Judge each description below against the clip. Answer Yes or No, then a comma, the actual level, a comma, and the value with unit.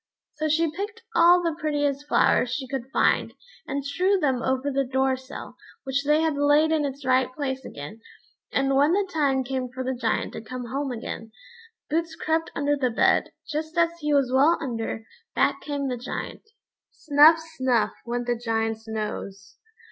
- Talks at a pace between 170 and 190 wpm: Yes, average, 180 wpm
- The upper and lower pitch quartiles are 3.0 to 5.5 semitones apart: Yes, average, 3.3 semitones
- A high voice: Yes, very high, 275 Hz